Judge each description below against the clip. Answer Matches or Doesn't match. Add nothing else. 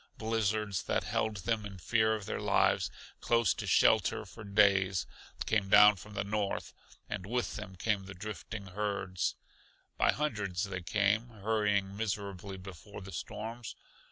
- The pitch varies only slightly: Matches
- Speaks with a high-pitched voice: Doesn't match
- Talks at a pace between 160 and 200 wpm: Doesn't match